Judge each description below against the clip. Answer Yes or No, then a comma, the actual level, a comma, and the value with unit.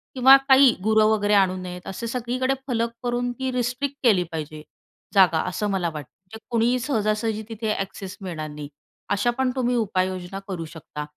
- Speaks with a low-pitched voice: No, high, 215 Hz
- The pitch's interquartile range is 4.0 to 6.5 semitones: Yes, average, 4.9 semitones